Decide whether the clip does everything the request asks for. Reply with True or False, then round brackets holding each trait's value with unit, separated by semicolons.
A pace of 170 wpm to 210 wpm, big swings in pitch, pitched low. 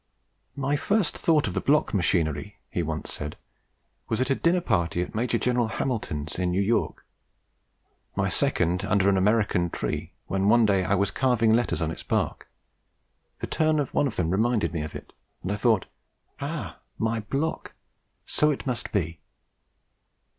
True (175 wpm; 5.9 semitones; 105 Hz)